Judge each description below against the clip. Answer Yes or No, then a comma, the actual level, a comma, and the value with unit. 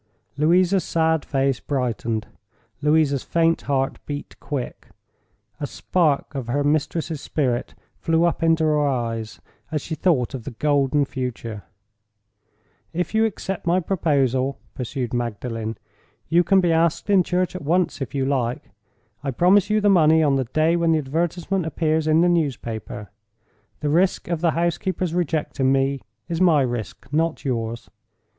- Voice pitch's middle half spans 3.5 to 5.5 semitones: Yes, average, 4.2 semitones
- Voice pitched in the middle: Yes, medium, 150 Hz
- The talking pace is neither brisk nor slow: Yes, average, 150 wpm